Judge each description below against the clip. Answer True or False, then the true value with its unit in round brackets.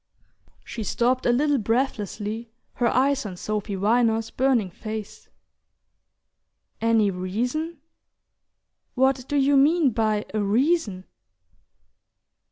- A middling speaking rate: False (100 wpm)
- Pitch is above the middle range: True (230 Hz)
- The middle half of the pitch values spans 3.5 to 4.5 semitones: True (4.1 semitones)